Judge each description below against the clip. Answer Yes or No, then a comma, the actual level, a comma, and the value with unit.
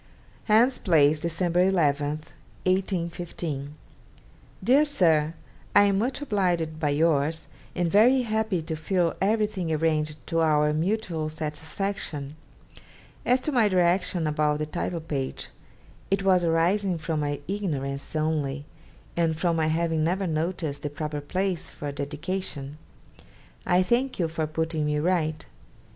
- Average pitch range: Yes, average, 3.7 semitones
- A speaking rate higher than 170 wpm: No, slow, 135 wpm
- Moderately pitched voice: Yes, medium, 165 Hz